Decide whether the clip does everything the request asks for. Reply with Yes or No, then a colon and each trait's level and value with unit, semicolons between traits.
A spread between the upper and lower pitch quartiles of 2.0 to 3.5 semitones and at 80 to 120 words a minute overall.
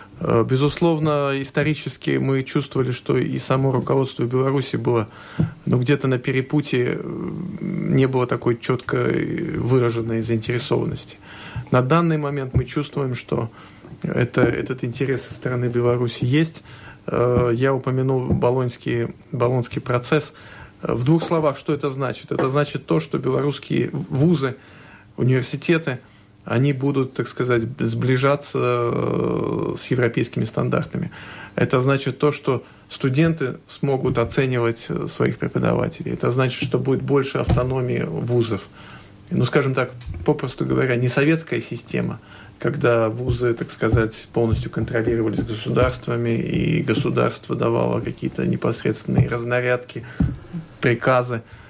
Yes: average, 3.2 semitones; average, 115 wpm